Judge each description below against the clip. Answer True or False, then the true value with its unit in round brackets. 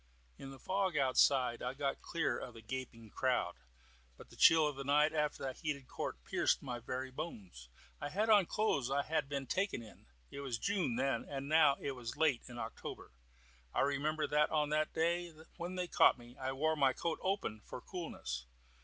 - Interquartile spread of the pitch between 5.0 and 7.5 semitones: False (3.8 semitones)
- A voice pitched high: False (140 Hz)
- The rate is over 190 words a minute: True (200 wpm)